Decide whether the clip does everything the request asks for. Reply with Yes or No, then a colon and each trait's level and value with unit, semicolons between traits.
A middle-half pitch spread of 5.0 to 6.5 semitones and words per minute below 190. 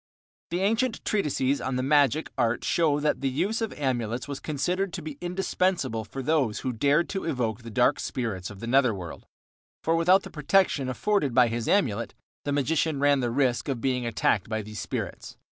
No: wide, 5.4 semitones; average, 195 wpm